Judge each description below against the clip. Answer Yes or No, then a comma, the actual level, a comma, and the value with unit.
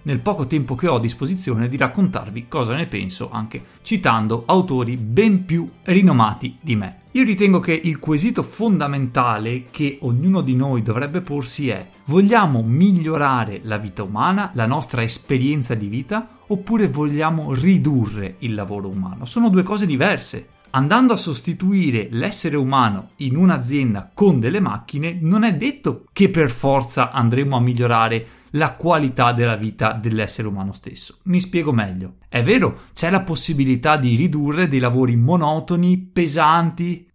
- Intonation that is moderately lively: No, wide, 6.9 semitones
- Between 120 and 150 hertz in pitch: Yes, medium, 140 Hz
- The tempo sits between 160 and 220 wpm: No, average, 150 wpm